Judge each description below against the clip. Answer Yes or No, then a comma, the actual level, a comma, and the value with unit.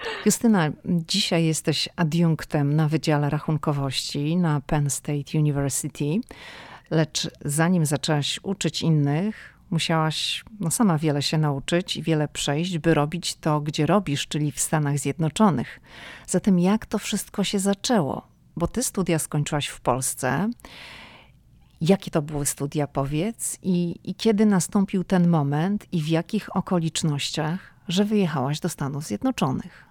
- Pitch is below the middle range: No, medium, 160 Hz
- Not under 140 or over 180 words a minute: No, average, 130 wpm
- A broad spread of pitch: No, average, 4.0 semitones